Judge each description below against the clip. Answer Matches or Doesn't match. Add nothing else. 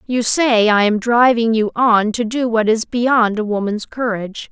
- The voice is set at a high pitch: Matches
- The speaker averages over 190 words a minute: Matches